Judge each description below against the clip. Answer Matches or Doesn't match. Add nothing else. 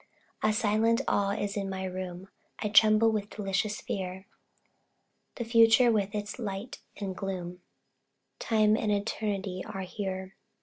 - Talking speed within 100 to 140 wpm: Matches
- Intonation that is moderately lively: Doesn't match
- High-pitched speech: Matches